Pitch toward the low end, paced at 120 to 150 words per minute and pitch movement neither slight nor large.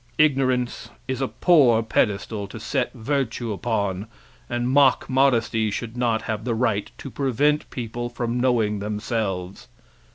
Yes: low, 120 Hz; slow, 135 wpm; average, 3.0 semitones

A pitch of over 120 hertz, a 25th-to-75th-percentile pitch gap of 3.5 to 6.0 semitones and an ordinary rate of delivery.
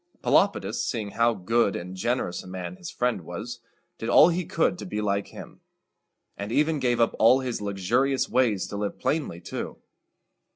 No: low, 115 Hz; average, 4.6 semitones; average, 175 wpm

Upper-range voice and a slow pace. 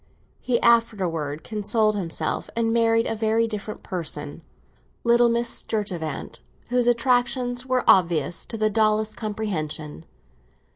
Yes: high, 215 Hz; slow, 115 wpm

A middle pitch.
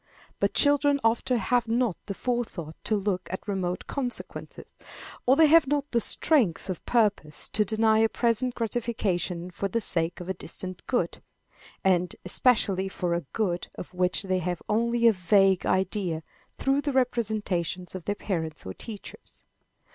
No: high, 205 Hz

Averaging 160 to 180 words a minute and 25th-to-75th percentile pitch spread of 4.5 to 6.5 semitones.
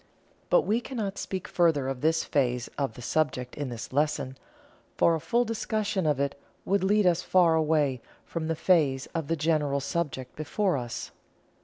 Yes: average, 175 wpm; average, 5.1 semitones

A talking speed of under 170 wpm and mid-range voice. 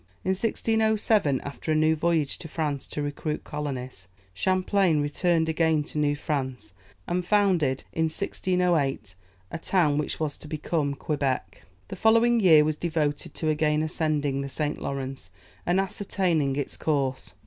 Yes: average, 150 wpm; medium, 155 Hz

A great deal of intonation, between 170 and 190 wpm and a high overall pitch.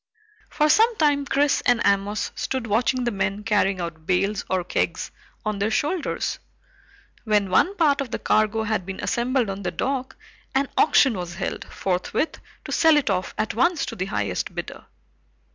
Yes: wide, 6.2 semitones; average, 175 wpm; high, 220 Hz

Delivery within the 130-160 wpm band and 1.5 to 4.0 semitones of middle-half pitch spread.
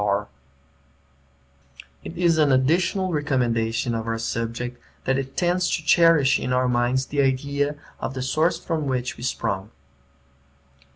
No: average, 150 wpm; average, 4.5 semitones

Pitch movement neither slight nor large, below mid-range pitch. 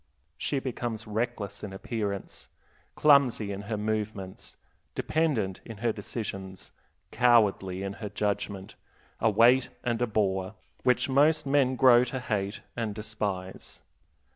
Yes: average, 3.6 semitones; low, 110 Hz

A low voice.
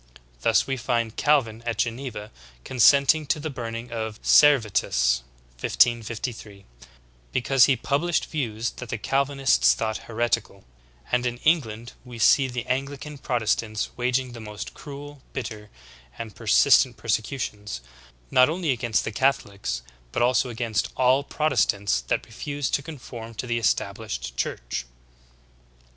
Yes: low, 120 Hz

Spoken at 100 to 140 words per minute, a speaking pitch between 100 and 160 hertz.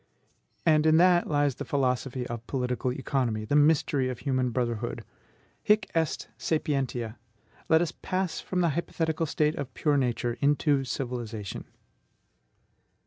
Yes: slow, 135 wpm; medium, 140 Hz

